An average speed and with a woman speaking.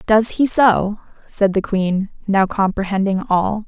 Yes: average, 145 wpm; female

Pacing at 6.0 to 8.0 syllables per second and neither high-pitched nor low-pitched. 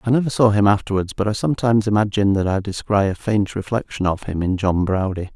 No: 6.3 syllables/s; low, 100 Hz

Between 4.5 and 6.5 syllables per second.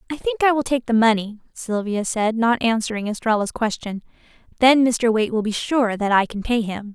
Yes: 5.4 syllables/s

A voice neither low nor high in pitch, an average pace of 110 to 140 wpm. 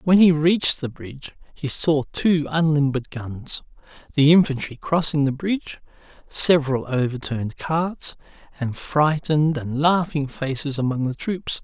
Yes: medium, 150 Hz; slow, 135 wpm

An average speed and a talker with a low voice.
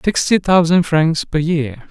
No: average, 155 wpm; medium, 160 Hz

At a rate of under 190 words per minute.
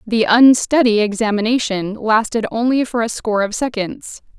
Yes: slow, 135 wpm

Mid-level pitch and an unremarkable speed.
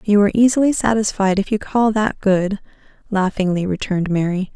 No: high, 200 Hz; average, 160 wpm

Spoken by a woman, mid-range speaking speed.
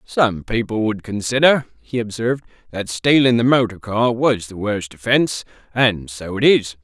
No: male; average, 165 wpm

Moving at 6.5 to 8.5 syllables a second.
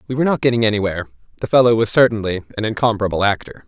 Yes: 8.3 syllables/s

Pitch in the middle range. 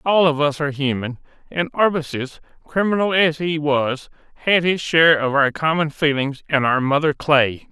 Yes: medium, 150 Hz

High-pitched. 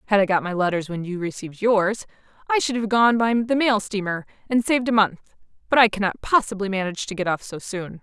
Yes: high, 205 Hz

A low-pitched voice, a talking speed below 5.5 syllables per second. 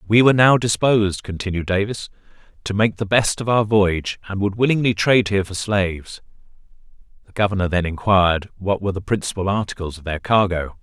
No: low, 100 Hz; 6.1 syllables/s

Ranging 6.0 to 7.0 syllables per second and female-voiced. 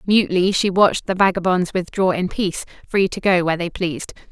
Yes: 6.1 syllables/s; female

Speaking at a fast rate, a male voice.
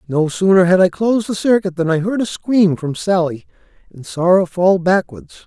Yes: fast, 210 wpm; male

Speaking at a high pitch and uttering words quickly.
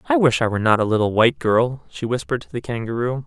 No: low, 125 Hz; fast, 255 wpm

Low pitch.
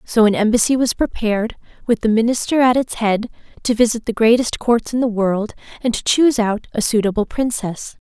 No: high, 230 Hz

